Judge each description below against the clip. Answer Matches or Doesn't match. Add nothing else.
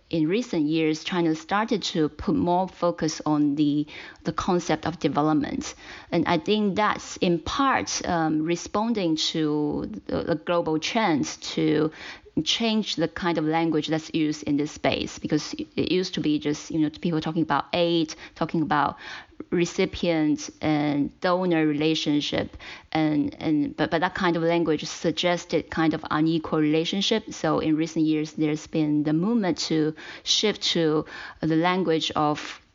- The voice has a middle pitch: Matches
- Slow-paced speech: Doesn't match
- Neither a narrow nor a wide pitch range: Doesn't match